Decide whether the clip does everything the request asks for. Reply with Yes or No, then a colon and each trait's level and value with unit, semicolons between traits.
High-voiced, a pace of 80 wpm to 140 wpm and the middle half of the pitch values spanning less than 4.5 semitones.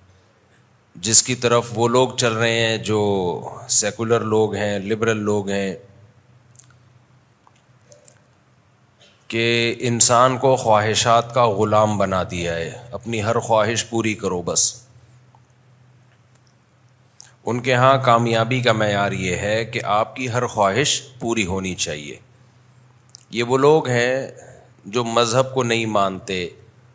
No: low, 115 Hz; average, 120 wpm; narrow, 2.6 semitones